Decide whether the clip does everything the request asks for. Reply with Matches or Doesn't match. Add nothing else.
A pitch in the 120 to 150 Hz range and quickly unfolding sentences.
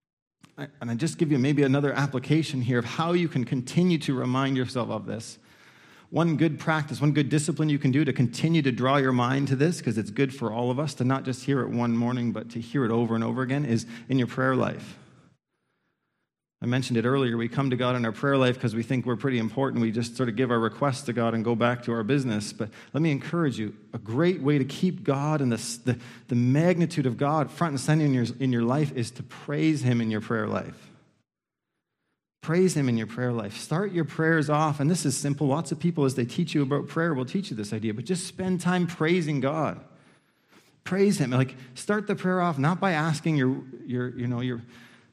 Matches